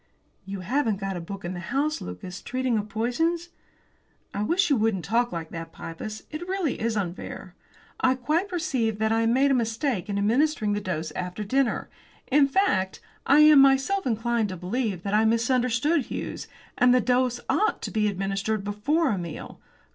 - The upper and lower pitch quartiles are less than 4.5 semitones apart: No, wide, 5.6 semitones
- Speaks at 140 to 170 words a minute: No, average, 185 wpm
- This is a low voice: No, high, 225 Hz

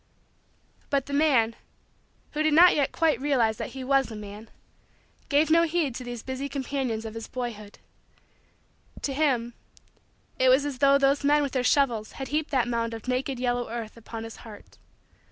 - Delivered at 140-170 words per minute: No, average, 180 wpm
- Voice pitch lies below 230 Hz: No, very high, 260 Hz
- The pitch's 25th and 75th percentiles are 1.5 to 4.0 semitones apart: Yes, average, 3.6 semitones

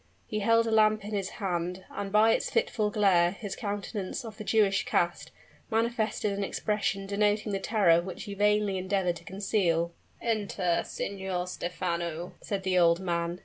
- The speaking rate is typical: Yes, average, 165 wpm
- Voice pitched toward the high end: Yes, high, 200 Hz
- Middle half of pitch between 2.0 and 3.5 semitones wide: Yes, average, 2.8 semitones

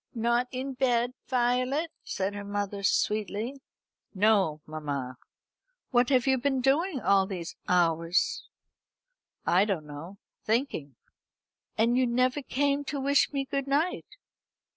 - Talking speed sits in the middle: No, slow, 125 wpm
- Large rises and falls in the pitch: Yes, wide, 5.8 semitones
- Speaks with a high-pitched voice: Yes, high, 235 Hz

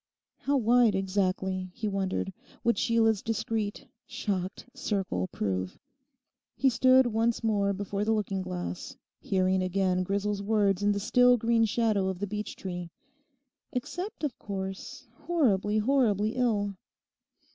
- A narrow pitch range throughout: No, average, 3.2 semitones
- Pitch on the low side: No, high, 205 Hz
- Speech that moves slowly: Yes, slow, 130 wpm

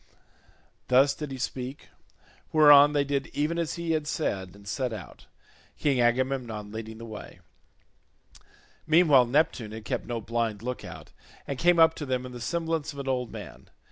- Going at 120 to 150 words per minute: No, average, 170 wpm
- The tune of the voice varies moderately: Yes, average, 4.3 semitones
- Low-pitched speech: Yes, low, 130 Hz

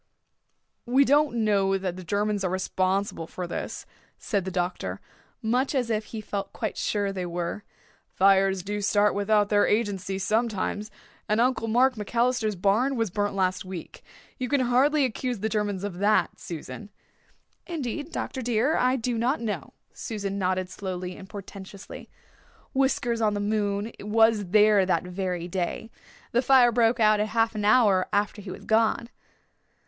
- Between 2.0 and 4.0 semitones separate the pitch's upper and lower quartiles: Yes, average, 3.3 semitones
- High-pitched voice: Yes, high, 210 Hz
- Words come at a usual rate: Yes, average, 160 wpm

